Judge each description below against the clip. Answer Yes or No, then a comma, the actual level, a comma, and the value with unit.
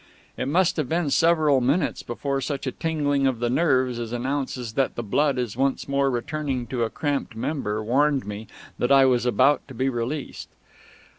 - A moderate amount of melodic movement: Yes, average, 3.0 semitones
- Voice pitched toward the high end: No, low, 135 Hz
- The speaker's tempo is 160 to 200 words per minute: Yes, average, 190 wpm